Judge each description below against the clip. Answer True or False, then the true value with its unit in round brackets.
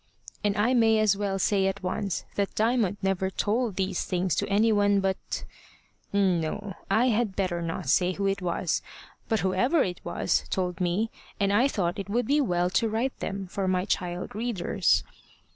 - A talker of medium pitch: False (195 Hz)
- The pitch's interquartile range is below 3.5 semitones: True (2.8 semitones)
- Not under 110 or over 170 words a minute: False (180 wpm)